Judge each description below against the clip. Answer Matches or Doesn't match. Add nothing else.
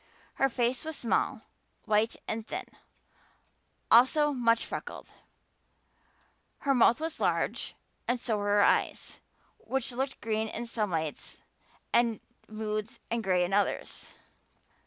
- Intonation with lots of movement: Doesn't match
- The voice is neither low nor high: Doesn't match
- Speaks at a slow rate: Matches